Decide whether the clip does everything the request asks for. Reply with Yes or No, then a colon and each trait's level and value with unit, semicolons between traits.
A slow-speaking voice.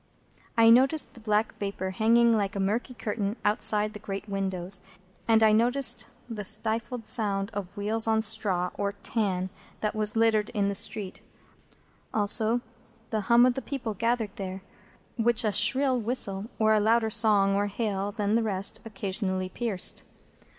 No: average, 165 wpm